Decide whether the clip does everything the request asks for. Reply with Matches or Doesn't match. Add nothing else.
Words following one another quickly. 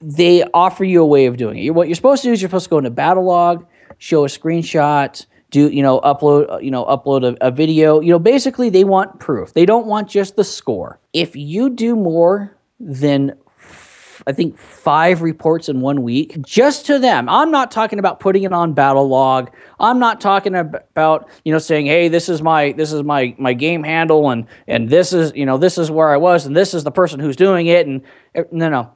Matches